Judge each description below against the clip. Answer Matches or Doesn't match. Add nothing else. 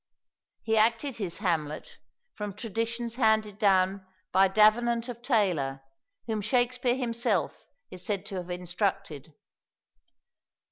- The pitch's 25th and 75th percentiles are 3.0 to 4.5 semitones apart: Matches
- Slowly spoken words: Matches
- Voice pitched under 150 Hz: Doesn't match